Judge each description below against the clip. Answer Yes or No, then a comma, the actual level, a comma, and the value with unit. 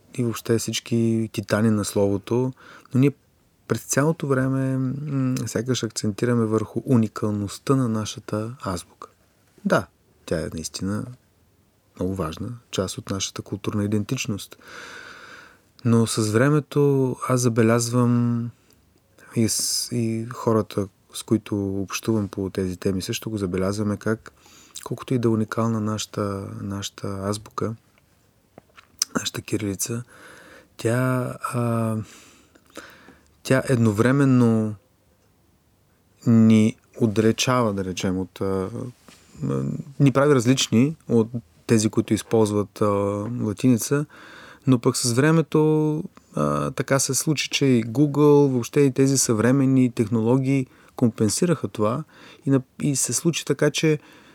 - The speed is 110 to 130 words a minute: Yes, slow, 115 wpm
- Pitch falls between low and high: No, low, 115 Hz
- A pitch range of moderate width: Yes, average, 4.0 semitones